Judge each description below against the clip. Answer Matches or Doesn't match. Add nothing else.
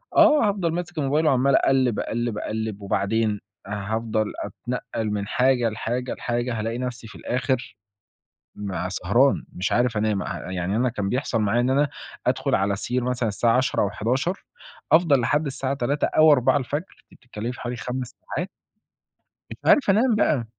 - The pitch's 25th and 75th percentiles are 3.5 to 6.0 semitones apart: Matches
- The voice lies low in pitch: Matches